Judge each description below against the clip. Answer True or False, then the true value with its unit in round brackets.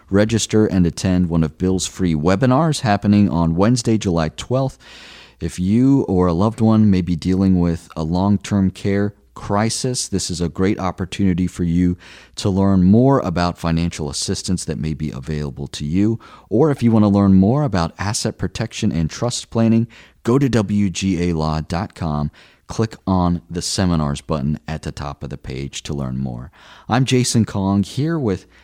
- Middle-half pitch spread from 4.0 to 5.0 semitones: True (4.5 semitones)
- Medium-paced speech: True (170 wpm)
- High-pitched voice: False (95 Hz)